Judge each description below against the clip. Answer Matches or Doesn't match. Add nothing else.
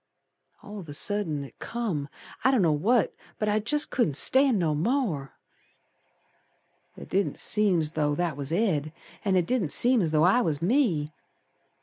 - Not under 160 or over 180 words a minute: Matches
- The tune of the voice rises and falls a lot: Matches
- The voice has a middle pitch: Matches